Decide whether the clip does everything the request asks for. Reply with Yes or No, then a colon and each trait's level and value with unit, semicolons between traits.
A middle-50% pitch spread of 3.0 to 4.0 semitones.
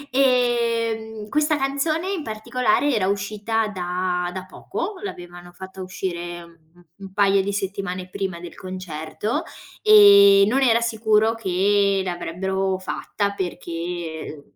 Yes: average, 3.7 semitones